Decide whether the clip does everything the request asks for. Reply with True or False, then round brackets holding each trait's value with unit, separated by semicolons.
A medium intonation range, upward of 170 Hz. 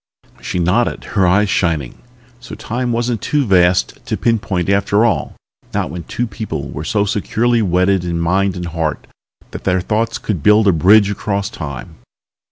False (3.7 semitones; 100 Hz)